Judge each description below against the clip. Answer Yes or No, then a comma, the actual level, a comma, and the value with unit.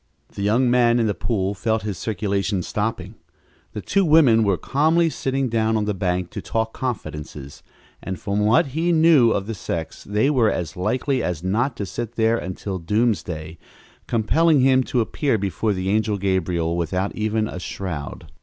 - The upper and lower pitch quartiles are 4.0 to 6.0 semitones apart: Yes, average, 4.4 semitones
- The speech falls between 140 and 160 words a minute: No, average, 175 wpm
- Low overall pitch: Yes, low, 110 Hz